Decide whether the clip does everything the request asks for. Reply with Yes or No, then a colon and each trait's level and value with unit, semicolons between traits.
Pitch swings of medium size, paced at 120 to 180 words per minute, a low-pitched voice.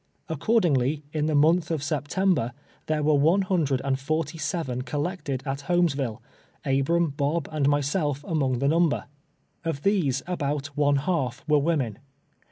No: average, 3.1 semitones; average, 150 wpm; medium, 150 Hz